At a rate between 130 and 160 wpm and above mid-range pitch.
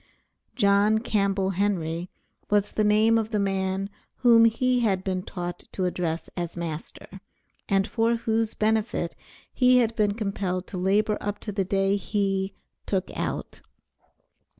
Yes: average, 145 wpm; high, 200 Hz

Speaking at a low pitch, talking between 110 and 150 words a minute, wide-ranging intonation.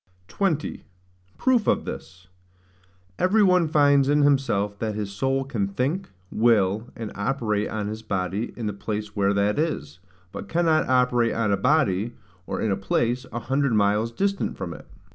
No: low, 115 Hz; average, 165 wpm; wide, 5.8 semitones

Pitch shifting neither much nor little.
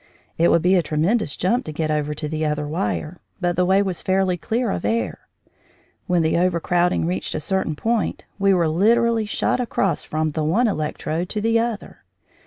Yes: average, 4.9 semitones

